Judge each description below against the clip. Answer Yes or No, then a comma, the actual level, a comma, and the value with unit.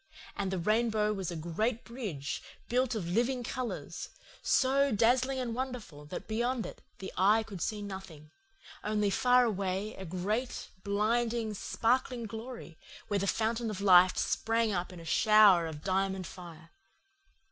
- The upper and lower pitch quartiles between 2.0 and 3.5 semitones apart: No, average, 4.0 semitones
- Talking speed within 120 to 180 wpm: Yes, average, 150 wpm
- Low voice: No, high, 215 Hz